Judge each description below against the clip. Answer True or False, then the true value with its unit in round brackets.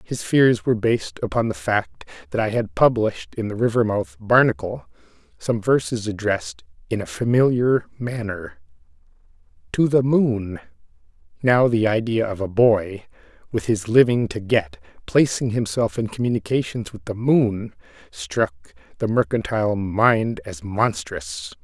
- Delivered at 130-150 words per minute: True (135 wpm)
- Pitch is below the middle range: True (115 Hz)